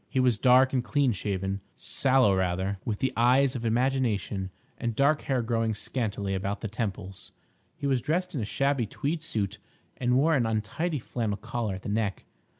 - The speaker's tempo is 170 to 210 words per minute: Yes, average, 180 wpm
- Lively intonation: No, average, 4.6 semitones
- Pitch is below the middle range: Yes, low, 115 Hz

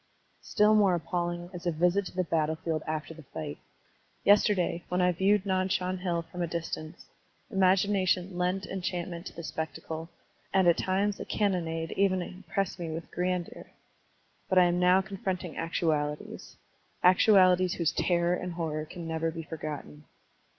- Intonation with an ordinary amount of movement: No, narrow, 2.3 semitones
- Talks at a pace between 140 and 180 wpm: Yes, average, 160 wpm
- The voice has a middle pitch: Yes, medium, 175 Hz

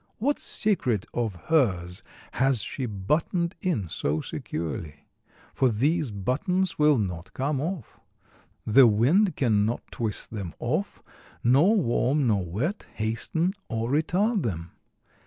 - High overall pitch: No, low, 125 Hz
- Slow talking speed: Yes, slow, 125 wpm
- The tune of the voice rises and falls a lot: Yes, wide, 7.8 semitones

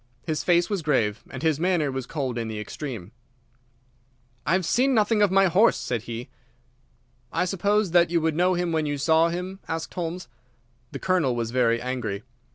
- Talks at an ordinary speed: Yes, average, 185 wpm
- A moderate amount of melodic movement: No, wide, 6.3 semitones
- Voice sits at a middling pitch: Yes, medium, 160 Hz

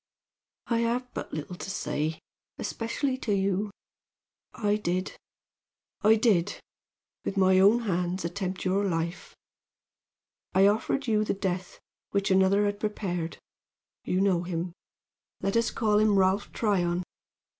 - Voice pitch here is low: No, high, 195 Hz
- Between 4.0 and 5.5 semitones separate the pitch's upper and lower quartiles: No, average, 2.8 semitones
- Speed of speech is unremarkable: No, slow, 130 wpm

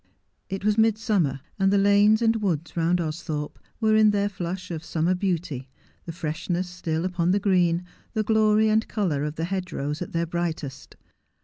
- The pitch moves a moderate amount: Yes, average, 3.8 semitones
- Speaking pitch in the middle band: Yes, medium, 180 Hz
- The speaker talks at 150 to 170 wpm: No, average, 180 wpm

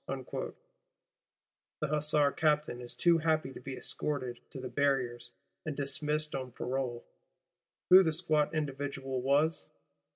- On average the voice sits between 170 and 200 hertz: No, medium, 145 Hz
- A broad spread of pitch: No, average, 2.8 semitones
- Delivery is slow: Yes, slow, 125 wpm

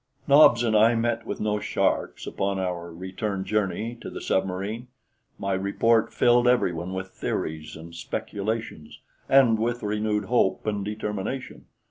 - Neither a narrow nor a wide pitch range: Yes, average, 3.5 semitones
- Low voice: Yes, low, 105 Hz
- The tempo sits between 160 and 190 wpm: No, average, 140 wpm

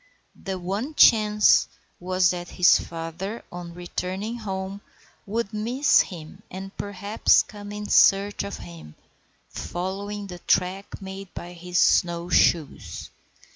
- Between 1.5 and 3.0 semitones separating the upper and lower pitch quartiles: Yes, narrow, 2.6 semitones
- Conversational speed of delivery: No, slow, 125 wpm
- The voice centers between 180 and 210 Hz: Yes, high, 190 Hz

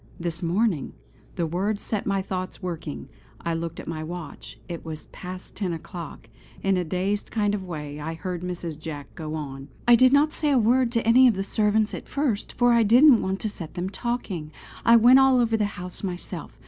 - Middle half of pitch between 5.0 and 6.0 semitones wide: Yes, average, 5.3 semitones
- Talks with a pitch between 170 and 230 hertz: Yes, high, 190 Hz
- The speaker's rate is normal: No, fast, 210 wpm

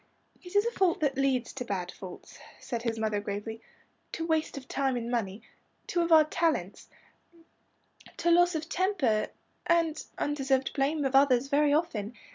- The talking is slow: No, average, 165 wpm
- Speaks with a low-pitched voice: No, very high, 275 Hz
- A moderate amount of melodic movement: No, wide, 5.9 semitones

